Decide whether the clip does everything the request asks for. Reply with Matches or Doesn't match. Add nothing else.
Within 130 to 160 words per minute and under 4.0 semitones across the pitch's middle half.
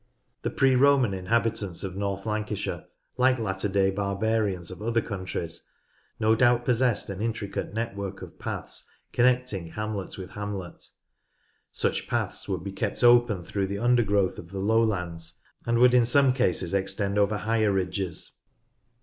Matches